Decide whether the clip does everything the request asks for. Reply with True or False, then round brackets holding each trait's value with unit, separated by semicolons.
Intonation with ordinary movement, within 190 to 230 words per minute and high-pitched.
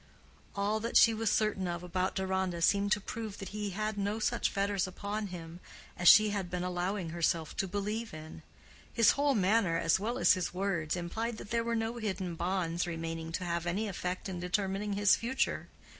True (3.3 semitones; 195 wpm; 195 Hz)